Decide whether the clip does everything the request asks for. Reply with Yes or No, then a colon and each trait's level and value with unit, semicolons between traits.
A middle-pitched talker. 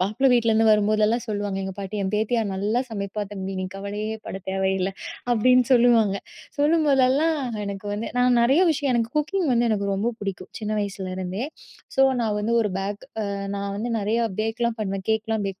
No: high, 215 Hz